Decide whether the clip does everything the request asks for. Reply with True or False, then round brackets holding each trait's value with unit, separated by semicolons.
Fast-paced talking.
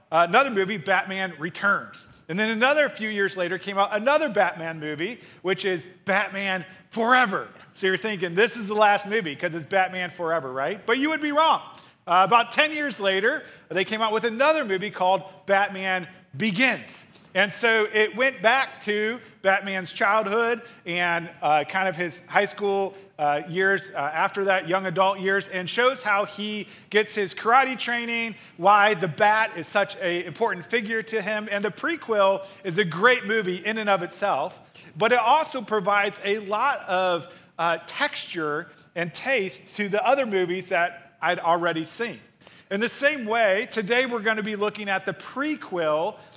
False (175 wpm)